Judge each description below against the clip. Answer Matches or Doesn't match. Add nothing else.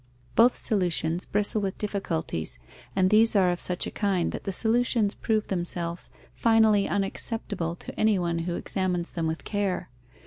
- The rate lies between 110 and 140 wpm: Doesn't match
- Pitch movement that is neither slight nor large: Matches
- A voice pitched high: Matches